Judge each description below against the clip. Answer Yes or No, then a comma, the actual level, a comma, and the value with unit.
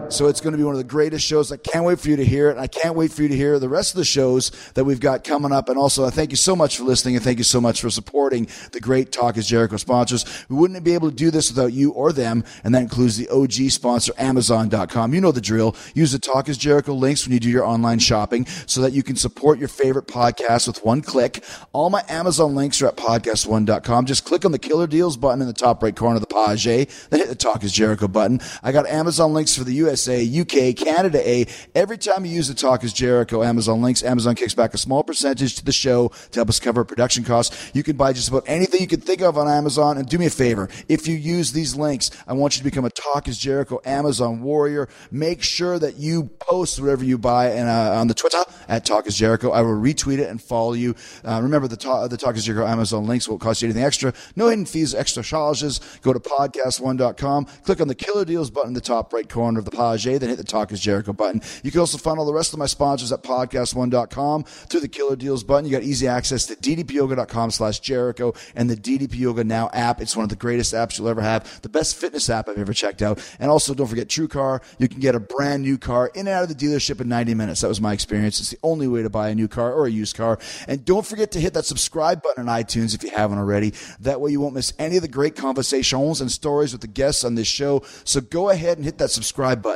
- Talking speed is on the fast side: Yes, fast, 265 wpm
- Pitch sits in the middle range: No, low, 130 Hz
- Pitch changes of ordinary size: Yes, average, 4.0 semitones